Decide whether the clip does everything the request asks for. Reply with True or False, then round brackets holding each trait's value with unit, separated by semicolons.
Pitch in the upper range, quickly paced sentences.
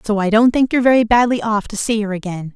True (220 Hz; 280 wpm)